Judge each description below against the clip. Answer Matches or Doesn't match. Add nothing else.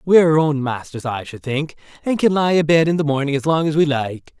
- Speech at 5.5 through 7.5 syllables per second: Matches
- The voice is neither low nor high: Matches